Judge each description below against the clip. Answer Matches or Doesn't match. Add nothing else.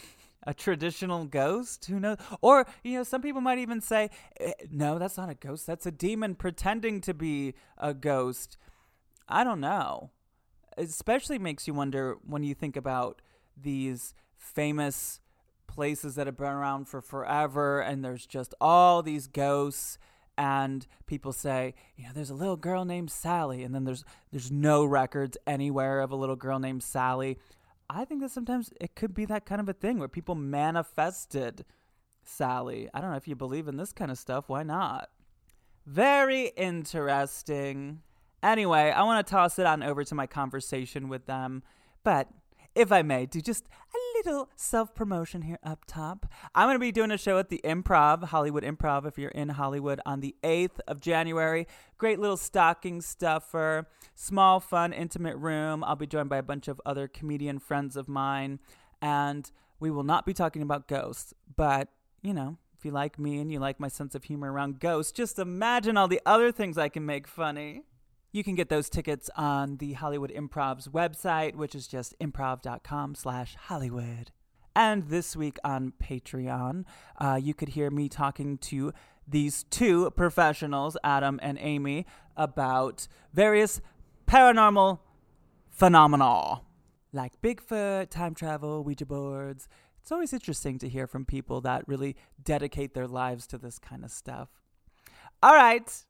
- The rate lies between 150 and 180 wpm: Matches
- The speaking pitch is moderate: Matches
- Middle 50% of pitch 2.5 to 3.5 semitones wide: Doesn't match